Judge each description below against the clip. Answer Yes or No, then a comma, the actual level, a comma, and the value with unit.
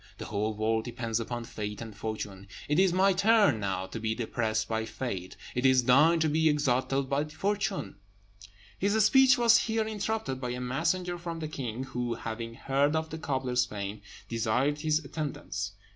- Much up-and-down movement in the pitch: Yes, wide, 6.4 semitones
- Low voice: Yes, low, 130 Hz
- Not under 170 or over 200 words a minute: Yes, average, 175 wpm